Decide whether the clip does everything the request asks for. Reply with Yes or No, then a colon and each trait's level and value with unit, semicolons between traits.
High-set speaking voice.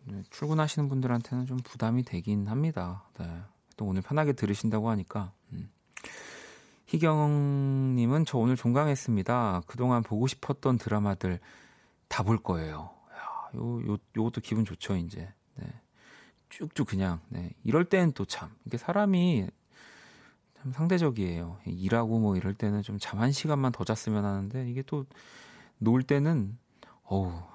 No: low, 115 Hz